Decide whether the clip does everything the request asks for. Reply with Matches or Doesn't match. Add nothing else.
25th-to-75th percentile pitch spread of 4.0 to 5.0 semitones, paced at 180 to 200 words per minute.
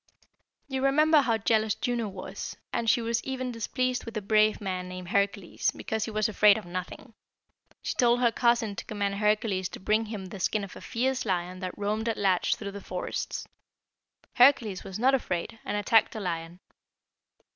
Doesn't match